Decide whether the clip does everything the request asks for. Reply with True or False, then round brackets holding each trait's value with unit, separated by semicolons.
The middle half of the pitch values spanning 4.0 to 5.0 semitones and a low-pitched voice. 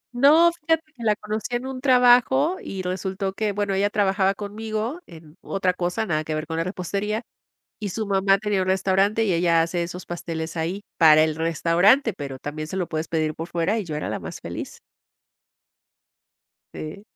False (4.5 semitones; 190 Hz)